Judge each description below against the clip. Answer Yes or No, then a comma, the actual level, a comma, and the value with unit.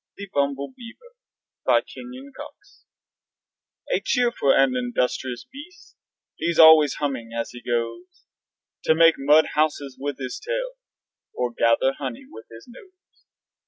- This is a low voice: No, medium, 145 Hz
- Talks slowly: Yes, slow, 125 wpm